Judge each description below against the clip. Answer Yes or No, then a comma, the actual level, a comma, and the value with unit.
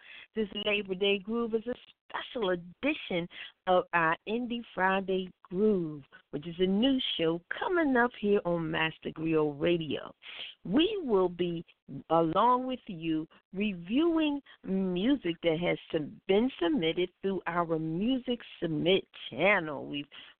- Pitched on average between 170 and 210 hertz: Yes, medium, 185 Hz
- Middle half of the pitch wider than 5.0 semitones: Yes, wide, 5.4 semitones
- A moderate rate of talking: No, slow, 125 wpm